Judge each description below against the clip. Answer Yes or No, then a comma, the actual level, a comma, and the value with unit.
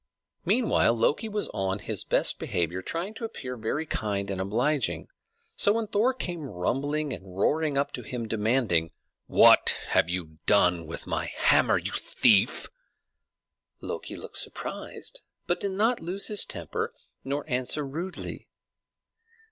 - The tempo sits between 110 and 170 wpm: Yes, average, 140 wpm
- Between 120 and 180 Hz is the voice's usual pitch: Yes, low, 135 Hz